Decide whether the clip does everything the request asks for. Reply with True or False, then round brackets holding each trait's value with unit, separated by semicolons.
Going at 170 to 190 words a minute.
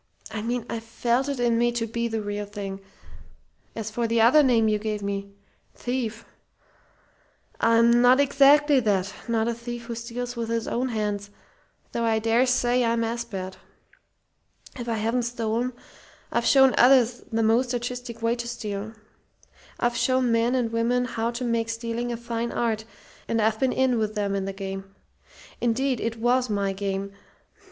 True (175 wpm)